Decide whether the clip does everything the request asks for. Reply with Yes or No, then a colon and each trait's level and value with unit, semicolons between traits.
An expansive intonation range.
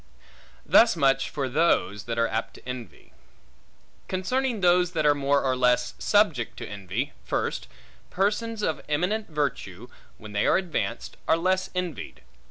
Yes: wide, 7.1 semitones